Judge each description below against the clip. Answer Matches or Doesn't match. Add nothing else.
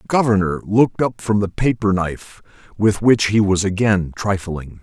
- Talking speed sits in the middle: Matches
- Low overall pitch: Matches